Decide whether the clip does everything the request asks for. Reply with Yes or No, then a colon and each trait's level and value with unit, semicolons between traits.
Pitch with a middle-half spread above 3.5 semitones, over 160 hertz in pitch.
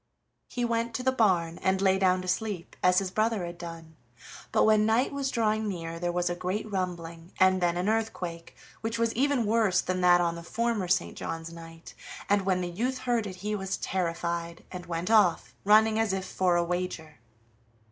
Yes: average, 4.0 semitones; medium, 185 Hz